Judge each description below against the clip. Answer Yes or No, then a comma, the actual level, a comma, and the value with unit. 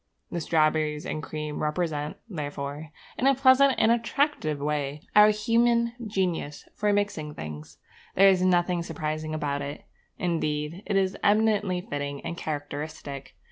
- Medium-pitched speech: Yes, medium, 160 Hz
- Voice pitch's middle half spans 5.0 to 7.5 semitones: Yes, wide, 5.4 semitones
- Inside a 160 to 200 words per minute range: No, average, 140 wpm